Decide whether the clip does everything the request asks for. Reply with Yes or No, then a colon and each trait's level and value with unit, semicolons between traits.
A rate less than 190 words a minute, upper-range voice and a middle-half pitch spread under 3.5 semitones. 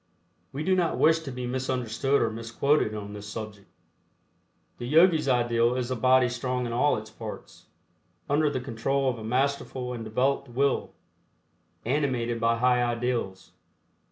No: average, 155 wpm; low, 125 Hz; average, 2.9 semitones